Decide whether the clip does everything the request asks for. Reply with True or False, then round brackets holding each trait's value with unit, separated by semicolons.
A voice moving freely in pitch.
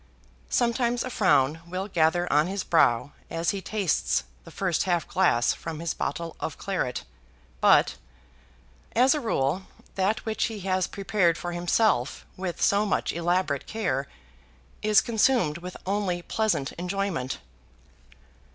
False (4.0 semitones)